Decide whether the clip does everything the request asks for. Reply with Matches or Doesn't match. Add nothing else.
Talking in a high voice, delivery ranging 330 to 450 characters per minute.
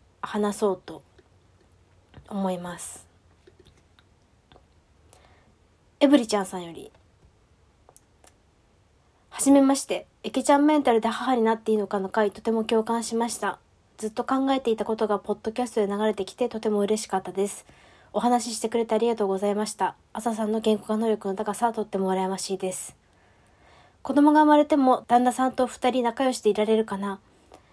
Matches